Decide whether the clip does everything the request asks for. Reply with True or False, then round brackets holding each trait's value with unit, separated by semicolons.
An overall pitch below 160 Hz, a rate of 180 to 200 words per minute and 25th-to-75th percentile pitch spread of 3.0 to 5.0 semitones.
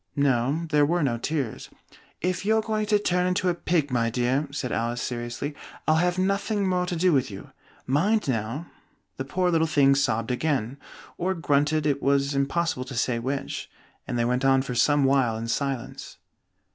False (140 Hz; 185 wpm; 5.6 semitones)